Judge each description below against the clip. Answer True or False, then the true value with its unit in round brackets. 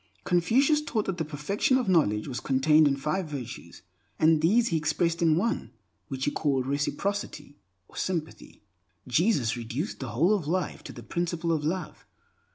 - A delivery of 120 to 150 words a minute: False (165 wpm)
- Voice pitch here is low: False (160 Hz)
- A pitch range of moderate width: True (4.8 semitones)